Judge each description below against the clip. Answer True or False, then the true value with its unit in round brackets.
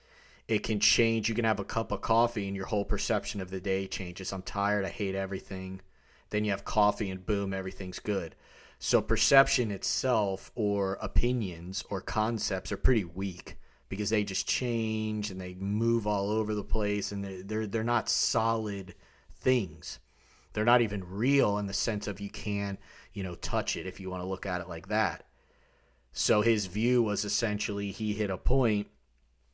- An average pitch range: False (2.3 semitones)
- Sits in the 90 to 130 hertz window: True (100 Hz)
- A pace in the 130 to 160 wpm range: False (185 wpm)